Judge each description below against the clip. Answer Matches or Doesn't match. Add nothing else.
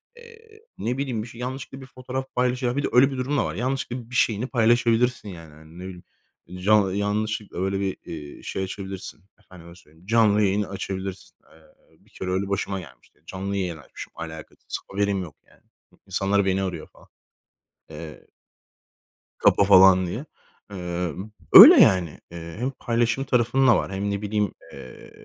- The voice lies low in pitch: Matches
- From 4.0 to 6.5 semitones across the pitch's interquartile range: Matches